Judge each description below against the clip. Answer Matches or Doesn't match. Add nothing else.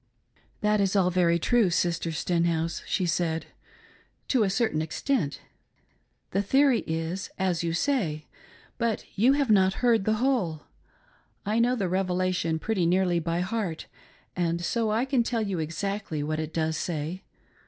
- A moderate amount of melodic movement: Matches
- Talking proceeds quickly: Doesn't match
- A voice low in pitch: Doesn't match